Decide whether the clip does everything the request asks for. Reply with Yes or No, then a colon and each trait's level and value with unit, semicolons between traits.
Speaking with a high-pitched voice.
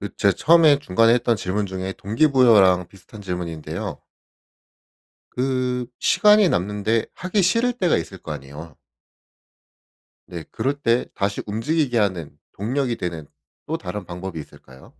No: low, 105 Hz